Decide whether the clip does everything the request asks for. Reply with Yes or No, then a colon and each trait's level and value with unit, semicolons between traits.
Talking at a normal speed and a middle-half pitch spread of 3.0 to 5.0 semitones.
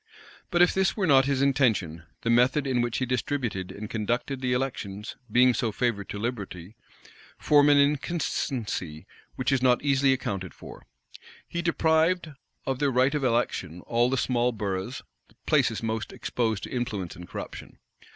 Yes: average, 165 wpm; average, 4.4 semitones